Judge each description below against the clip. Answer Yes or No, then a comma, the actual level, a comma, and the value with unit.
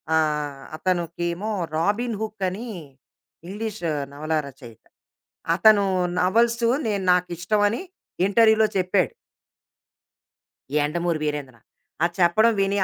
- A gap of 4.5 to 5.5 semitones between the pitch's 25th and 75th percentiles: Yes, average, 5.2 semitones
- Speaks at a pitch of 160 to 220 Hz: Yes, medium, 185 Hz